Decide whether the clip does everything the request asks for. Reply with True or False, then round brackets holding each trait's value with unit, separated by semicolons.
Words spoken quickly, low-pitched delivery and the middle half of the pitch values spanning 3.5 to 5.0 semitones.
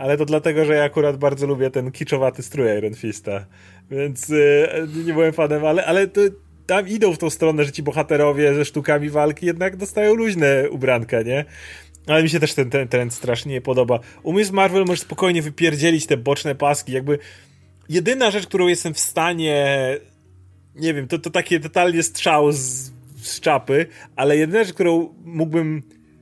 False (180 wpm; 150 Hz; 4.0 semitones)